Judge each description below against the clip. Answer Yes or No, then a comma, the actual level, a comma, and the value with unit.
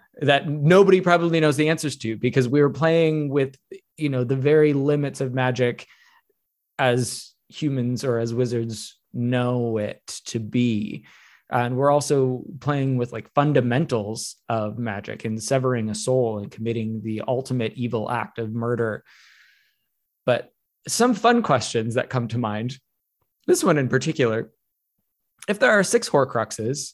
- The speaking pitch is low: Yes, low, 125 Hz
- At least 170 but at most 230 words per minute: No, average, 145 wpm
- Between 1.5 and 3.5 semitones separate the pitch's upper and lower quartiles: No, average, 4.1 semitones